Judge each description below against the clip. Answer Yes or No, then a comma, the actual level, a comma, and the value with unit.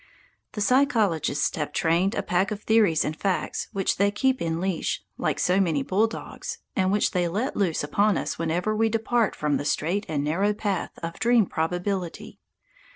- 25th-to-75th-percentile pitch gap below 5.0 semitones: Yes, average, 4.2 semitones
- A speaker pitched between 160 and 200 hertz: Yes, high, 190 Hz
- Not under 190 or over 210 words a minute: No, average, 175 wpm